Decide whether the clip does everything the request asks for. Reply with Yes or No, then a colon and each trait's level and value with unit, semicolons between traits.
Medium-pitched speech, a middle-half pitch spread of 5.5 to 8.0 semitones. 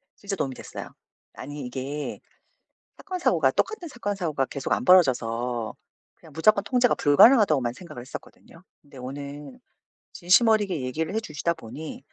Yes: medium, 155 Hz; wide, 7.2 semitones